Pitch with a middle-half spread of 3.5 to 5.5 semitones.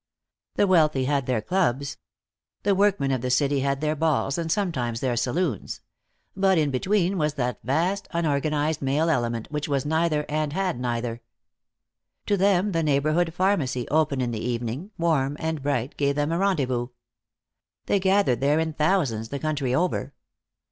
Yes: average, 4.5 semitones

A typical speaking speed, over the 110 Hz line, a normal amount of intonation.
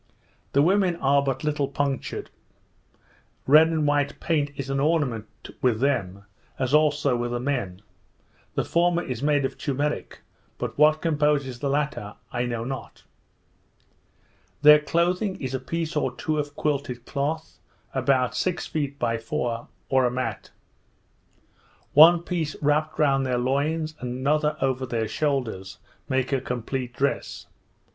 Yes: average, 145 wpm; medium, 140 Hz; average, 3.2 semitones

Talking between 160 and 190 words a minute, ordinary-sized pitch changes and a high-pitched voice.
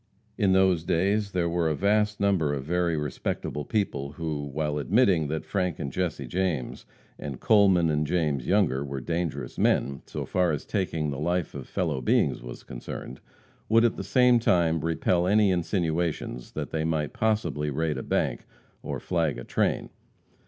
No: average, 170 wpm; average, 4.2 semitones; very low, 85 Hz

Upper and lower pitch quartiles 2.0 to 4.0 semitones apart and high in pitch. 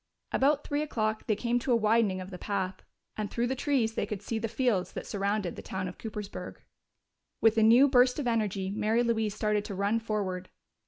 Yes: average, 2.8 semitones; high, 215 Hz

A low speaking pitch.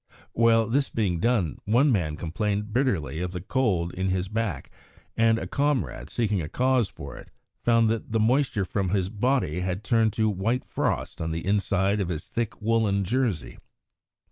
Yes: low, 105 Hz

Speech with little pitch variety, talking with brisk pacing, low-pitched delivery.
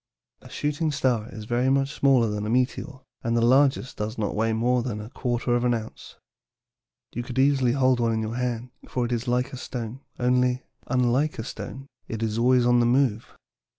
Yes: narrow, 2.1 semitones; fast, 210 wpm; low, 125 Hz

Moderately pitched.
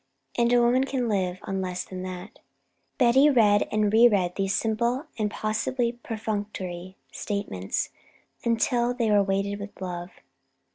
No: high, 210 Hz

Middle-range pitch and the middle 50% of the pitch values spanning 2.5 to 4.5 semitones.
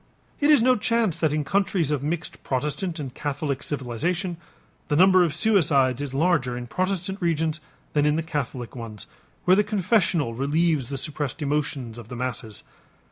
No: medium, 150 Hz; average, 5.3 semitones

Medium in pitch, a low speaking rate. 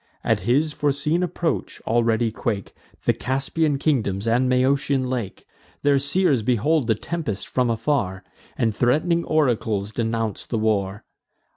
No: low, 125 Hz; slow, 130 wpm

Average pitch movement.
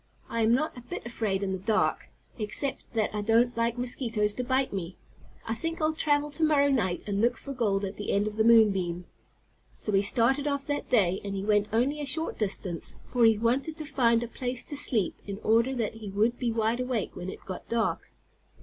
Yes: average, 4.0 semitones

